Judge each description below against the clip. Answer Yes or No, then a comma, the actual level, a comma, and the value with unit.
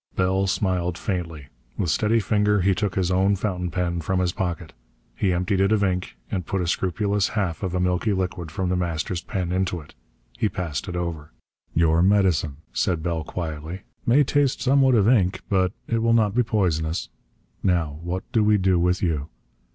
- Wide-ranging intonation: No, average, 2.8 semitones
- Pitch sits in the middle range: No, very low, 90 Hz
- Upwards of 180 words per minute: Yes, average, 190 wpm